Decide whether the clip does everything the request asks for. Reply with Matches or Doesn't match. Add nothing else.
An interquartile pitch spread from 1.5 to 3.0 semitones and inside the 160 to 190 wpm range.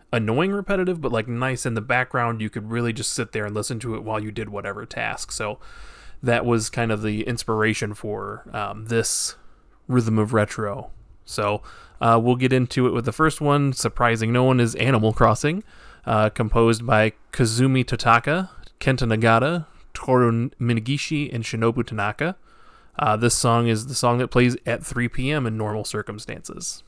Matches